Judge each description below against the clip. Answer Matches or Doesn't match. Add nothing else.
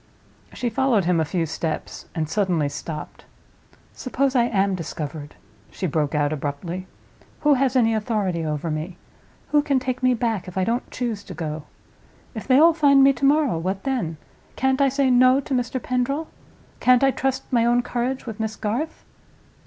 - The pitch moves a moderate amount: Doesn't match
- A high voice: Matches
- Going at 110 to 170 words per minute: Doesn't match